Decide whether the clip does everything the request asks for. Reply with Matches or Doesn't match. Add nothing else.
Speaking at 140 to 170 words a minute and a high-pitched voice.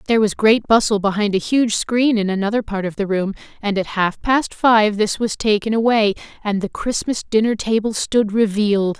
Doesn't match